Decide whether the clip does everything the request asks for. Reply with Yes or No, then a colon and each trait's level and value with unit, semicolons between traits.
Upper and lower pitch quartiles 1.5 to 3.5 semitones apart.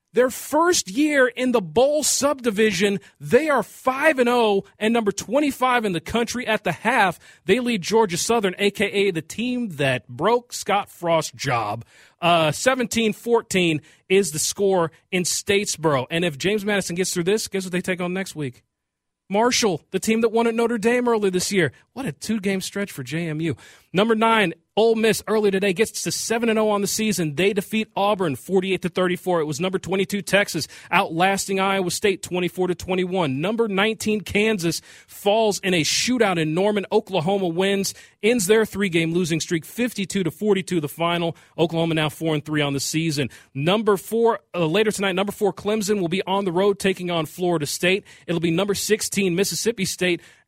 No: average, 4.1 semitones